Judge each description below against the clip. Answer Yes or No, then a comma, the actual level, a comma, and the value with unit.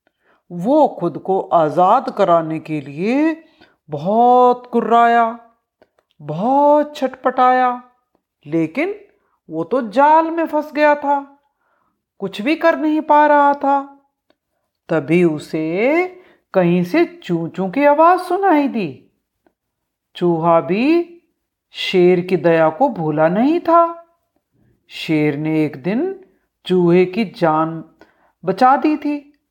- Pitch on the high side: Yes, very high, 250 Hz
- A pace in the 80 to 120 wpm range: Yes, slow, 110 wpm